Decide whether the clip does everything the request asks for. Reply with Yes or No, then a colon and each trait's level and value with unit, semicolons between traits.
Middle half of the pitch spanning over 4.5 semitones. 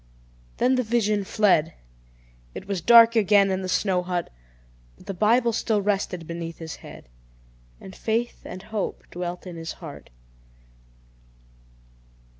No: average, 3.7 semitones